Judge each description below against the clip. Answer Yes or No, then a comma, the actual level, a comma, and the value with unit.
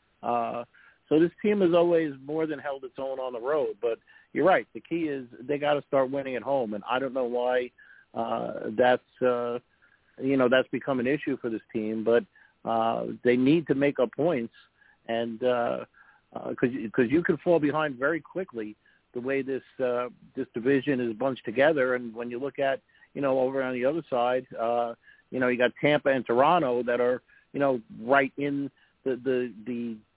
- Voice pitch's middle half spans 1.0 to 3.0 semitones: Yes, average, 2.7 semitones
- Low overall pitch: Yes, low, 130 Hz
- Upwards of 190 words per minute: Yes, average, 200 wpm